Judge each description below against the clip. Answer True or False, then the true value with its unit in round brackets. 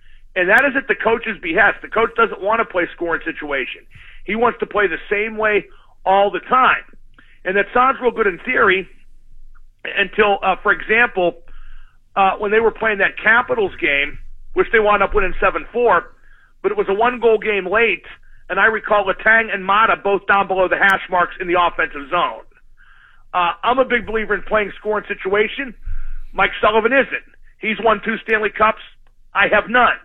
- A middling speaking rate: True (190 wpm)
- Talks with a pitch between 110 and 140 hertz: False (210 Hz)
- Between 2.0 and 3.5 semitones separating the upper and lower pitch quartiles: True (2.9 semitones)